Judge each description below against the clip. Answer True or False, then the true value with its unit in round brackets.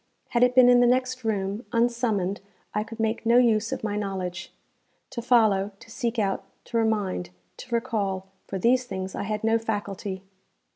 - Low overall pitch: False (220 Hz)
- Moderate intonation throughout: True (3.3 semitones)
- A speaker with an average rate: True (180 wpm)